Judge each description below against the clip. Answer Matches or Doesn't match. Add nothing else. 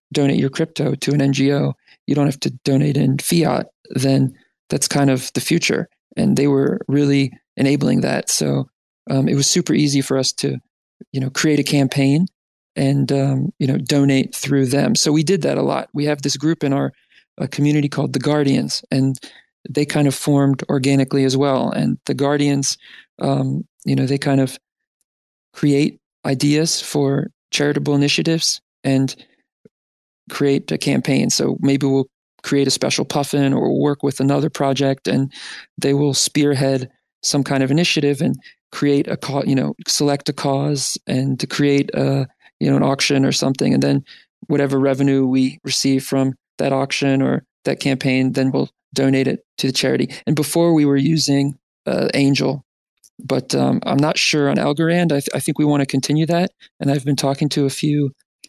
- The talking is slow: Doesn't match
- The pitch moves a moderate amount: Doesn't match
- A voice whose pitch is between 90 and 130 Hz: Doesn't match